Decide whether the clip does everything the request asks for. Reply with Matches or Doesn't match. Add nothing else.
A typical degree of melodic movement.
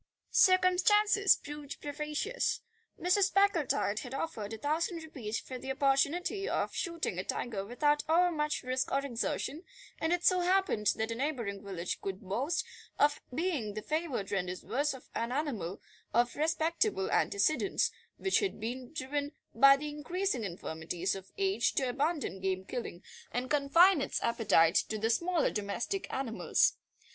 Doesn't match